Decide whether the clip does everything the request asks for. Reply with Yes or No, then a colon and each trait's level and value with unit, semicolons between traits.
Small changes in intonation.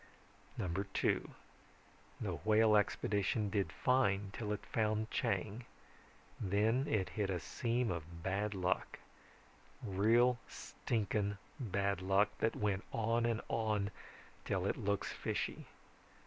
Yes: narrow, 2.3 semitones